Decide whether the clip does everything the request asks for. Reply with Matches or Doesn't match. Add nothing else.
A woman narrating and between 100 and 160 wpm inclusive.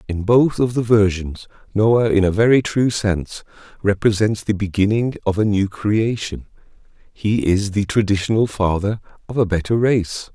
Doesn't match